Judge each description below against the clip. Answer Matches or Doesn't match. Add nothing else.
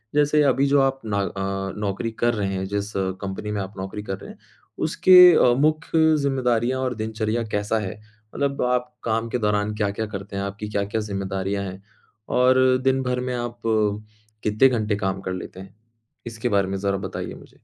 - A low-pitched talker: Matches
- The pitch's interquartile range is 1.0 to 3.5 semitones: Doesn't match